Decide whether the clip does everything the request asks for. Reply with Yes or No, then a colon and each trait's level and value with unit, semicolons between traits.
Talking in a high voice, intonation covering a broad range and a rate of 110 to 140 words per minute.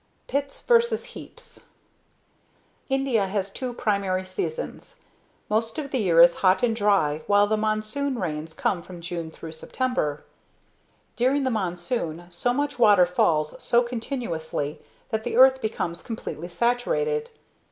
Yes: high, 215 Hz; wide, 6.7 semitones; slow, 135 wpm